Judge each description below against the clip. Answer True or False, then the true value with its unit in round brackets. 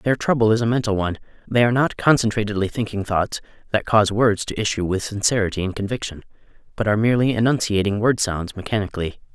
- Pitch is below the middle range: True (105 Hz)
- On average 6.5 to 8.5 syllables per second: True (6.7 syllables/s)